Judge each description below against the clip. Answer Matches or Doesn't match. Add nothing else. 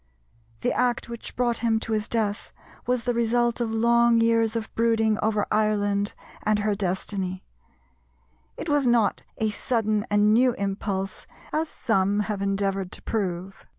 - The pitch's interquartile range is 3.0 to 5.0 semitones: Doesn't match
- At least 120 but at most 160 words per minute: Matches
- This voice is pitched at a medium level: Doesn't match